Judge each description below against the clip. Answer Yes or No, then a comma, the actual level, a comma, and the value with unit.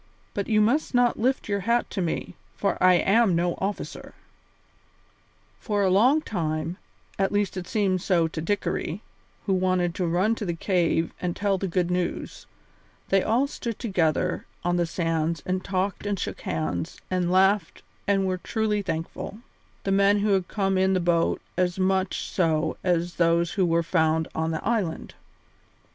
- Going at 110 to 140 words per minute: No, average, 170 wpm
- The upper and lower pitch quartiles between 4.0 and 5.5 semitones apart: No, average, 3.0 semitones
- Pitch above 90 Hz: Yes, medium, 185 Hz